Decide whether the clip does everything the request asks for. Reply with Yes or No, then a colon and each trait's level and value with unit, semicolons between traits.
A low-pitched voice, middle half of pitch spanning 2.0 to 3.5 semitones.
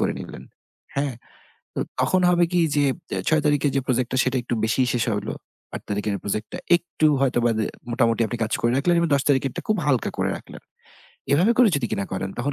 No: low, 130 Hz; average, 4.2 semitones